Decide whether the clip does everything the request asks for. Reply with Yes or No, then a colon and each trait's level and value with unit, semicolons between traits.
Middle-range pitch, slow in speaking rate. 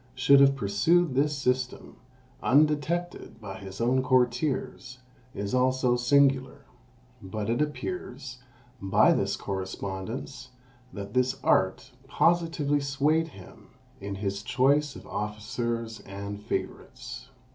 No: low, 125 Hz; slow, 110 wpm